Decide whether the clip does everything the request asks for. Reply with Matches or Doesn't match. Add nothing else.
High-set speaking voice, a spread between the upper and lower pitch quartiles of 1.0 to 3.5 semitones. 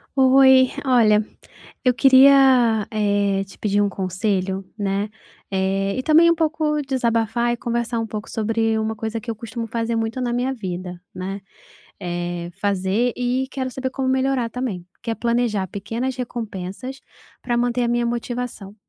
Doesn't match